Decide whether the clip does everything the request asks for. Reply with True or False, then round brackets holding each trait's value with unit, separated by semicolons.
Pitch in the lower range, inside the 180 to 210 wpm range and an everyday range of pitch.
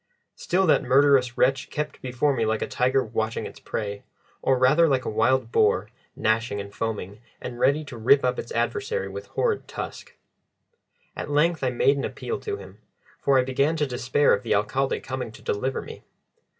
True (130 Hz; 190 wpm; 3.9 semitones)